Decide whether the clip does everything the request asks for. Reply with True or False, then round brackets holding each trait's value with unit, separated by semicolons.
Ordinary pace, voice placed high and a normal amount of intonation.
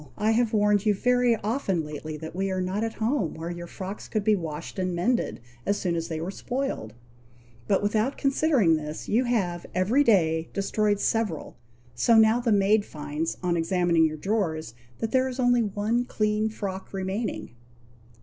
True (180 wpm; 200 Hz; 4.7 semitones)